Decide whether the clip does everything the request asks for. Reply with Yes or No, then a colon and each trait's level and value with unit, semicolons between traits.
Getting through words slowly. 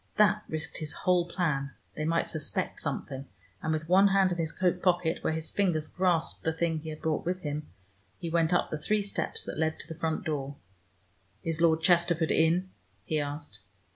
No: average, 200 wpm